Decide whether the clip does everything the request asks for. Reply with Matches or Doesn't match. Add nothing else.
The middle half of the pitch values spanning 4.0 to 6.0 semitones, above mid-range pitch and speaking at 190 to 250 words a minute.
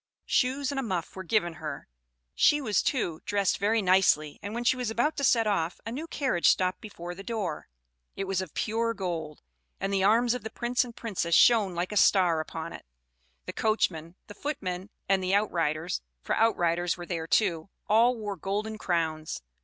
Matches